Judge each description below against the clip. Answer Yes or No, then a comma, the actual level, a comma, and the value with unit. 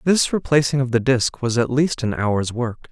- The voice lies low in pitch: Yes, low, 130 Hz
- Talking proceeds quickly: Yes, fast, 225 wpm